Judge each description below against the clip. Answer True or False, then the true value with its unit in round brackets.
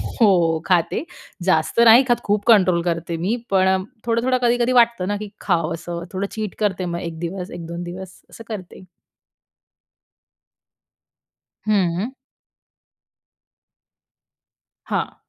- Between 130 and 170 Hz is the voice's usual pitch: False (190 Hz)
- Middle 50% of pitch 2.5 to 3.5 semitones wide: False (4.2 semitones)